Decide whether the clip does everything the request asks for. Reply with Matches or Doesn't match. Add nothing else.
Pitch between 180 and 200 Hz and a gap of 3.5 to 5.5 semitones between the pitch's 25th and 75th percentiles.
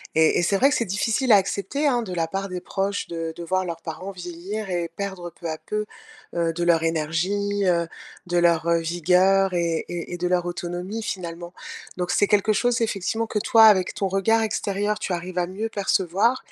Doesn't match